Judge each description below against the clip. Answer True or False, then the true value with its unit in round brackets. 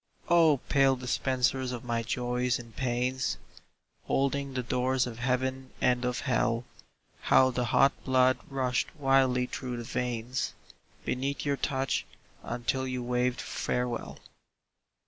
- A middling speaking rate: False (125 wpm)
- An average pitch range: False (1.3 semitones)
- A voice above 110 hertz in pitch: True (125 Hz)